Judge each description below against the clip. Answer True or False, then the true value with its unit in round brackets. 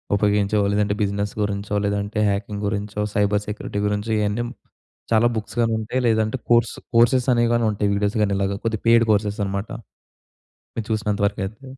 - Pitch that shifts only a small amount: True (1.6 semitones)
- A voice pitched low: True (105 Hz)